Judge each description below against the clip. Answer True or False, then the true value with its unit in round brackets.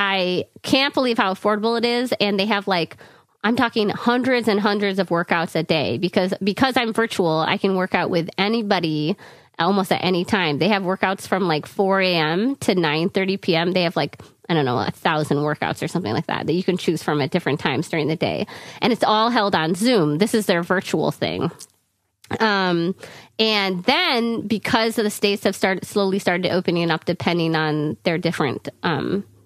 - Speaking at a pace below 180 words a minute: False (200 wpm)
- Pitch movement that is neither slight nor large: True (4.0 semitones)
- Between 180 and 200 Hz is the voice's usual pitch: True (190 Hz)